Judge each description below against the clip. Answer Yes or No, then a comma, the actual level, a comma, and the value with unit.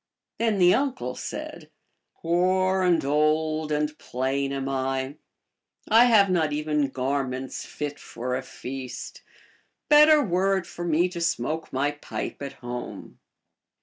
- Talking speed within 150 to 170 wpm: No, average, 140 wpm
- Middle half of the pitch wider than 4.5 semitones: Yes, average, 5.2 semitones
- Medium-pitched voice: Yes, medium, 150 Hz